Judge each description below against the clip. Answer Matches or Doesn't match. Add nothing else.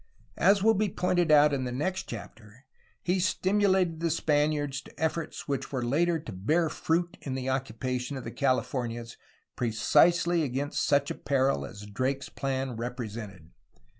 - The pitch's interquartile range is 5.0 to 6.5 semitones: Matches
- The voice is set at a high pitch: Doesn't match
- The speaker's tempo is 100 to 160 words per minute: Matches